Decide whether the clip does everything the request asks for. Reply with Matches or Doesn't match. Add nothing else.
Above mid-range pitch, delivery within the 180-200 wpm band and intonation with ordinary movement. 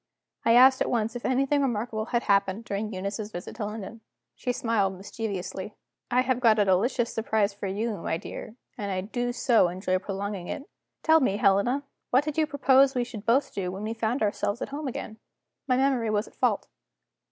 Matches